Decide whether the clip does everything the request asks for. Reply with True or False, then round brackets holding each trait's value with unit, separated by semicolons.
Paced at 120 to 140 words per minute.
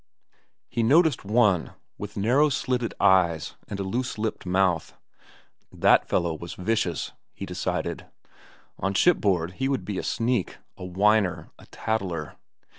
True (135 wpm)